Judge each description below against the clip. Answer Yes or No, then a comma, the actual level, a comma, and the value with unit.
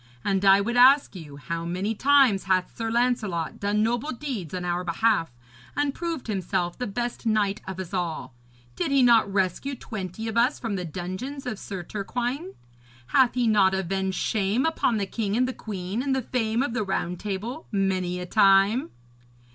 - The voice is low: No, high, 210 Hz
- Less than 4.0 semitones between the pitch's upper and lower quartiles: No, average, 4.6 semitones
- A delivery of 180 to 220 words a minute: Yes, average, 185 wpm